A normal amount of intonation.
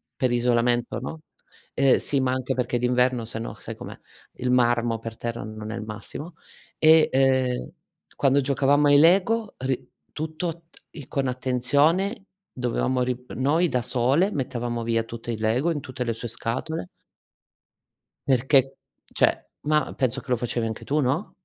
Yes: average, 3.2 semitones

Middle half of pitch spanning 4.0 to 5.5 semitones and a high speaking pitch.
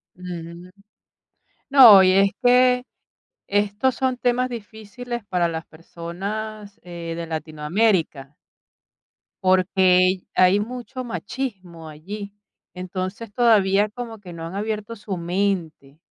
Yes: average, 4.3 semitones; high, 195 Hz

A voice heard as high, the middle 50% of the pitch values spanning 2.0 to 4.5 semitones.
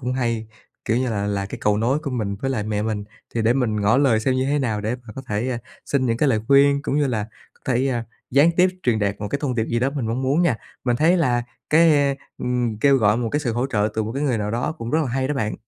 No: low, 125 Hz; average, 3.8 semitones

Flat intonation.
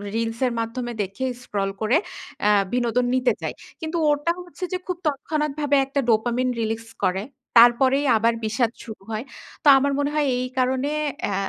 No: average, 3.9 semitones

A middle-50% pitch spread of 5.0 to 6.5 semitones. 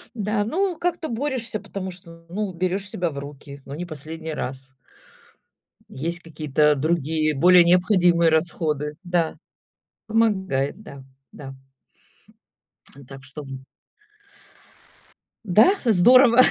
Yes: wide, 5.5 semitones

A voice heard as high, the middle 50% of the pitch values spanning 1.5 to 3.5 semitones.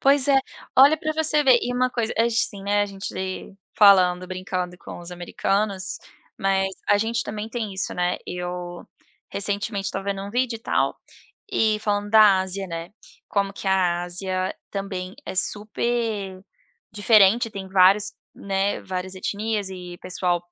Yes: high, 200 Hz; average, 2.8 semitones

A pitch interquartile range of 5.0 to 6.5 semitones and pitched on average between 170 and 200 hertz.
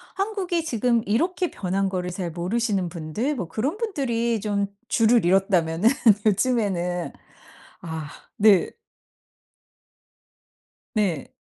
No: average, 5.3 semitones; high, 210 Hz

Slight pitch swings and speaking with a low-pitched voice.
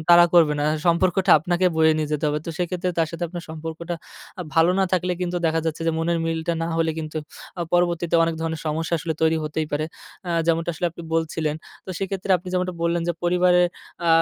No: narrow, 1.6 semitones; medium, 165 Hz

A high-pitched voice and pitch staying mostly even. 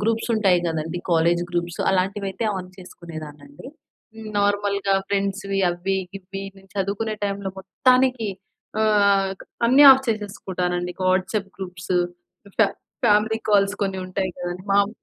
Yes: high, 195 Hz; narrow, 2.2 semitones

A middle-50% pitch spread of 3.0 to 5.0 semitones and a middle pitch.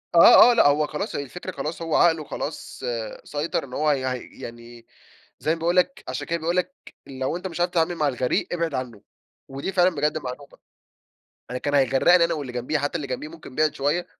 Yes: average, 4.1 semitones; medium, 150 Hz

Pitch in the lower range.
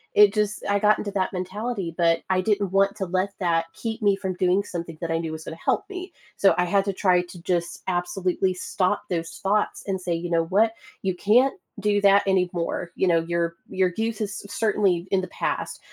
No: high, 190 Hz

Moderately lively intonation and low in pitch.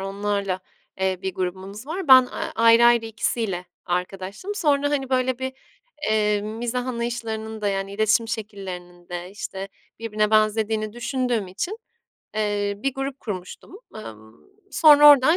No: average, 4.3 semitones; high, 215 Hz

